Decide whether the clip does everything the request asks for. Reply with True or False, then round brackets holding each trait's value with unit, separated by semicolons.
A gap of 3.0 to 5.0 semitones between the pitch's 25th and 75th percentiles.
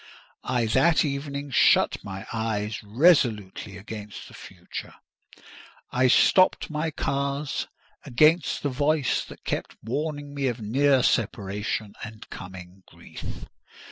False (5.4 semitones)